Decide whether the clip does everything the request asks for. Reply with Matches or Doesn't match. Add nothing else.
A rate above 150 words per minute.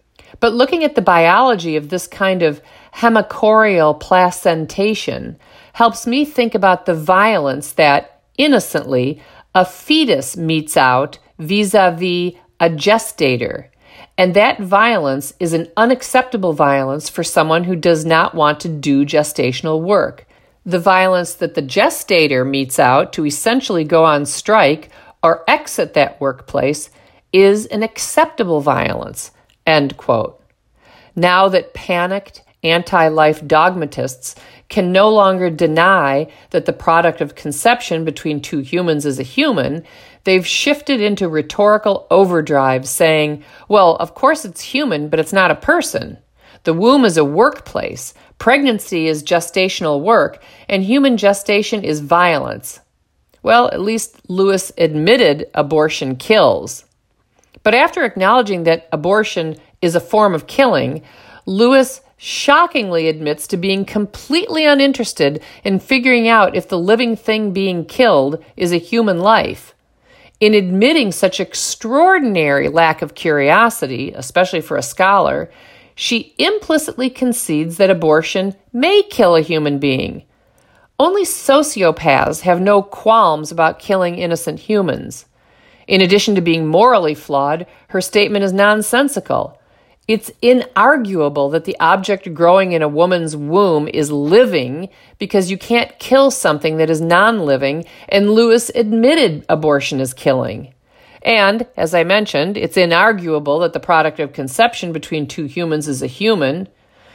Doesn't match